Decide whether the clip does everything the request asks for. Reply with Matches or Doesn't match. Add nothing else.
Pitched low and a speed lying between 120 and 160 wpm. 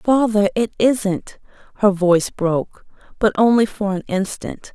Doesn't match